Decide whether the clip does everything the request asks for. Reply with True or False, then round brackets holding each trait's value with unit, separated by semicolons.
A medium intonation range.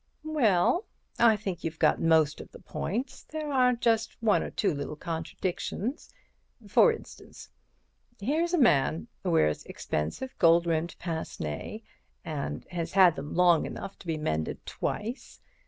False (6.7 semitones)